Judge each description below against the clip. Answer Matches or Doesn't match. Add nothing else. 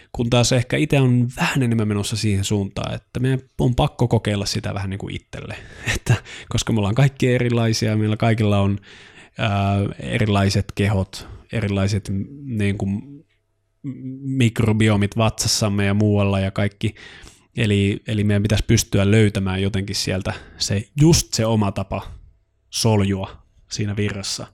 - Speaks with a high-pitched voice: Doesn't match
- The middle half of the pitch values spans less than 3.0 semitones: Matches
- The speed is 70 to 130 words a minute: Doesn't match